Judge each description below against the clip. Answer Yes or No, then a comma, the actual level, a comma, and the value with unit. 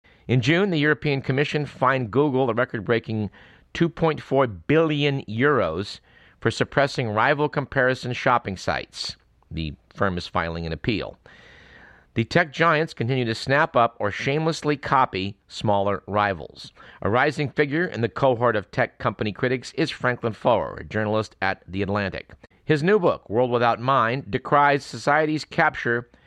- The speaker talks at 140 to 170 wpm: Yes, average, 145 wpm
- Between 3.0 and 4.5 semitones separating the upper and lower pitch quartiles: No, wide, 5.5 semitones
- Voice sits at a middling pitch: No, low, 125 Hz